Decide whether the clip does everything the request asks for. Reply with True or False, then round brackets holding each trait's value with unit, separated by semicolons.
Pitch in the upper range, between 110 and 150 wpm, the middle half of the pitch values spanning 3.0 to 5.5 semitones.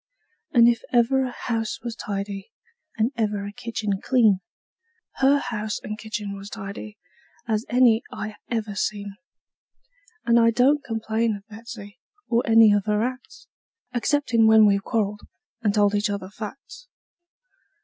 False (220 Hz; 145 wpm; 2.4 semitones)